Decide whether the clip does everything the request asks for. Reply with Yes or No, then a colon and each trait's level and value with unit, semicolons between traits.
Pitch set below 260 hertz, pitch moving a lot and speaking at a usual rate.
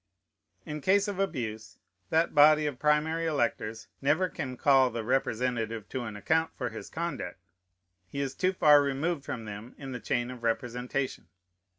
No: low, 135 Hz; average, 4.5 semitones; average, 165 wpm